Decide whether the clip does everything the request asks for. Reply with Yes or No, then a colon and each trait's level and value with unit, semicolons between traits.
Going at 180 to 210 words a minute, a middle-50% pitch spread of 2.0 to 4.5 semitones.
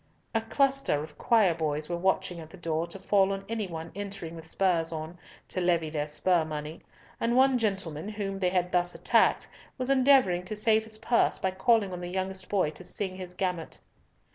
Yes: average, 200 wpm; average, 3.9 semitones